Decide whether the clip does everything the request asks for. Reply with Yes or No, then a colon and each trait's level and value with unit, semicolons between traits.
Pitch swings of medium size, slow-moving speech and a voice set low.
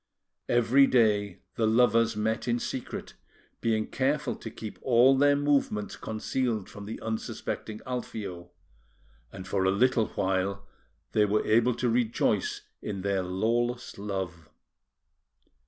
Yes: average, 3.4 semitones; slow, 125 wpm; low, 110 Hz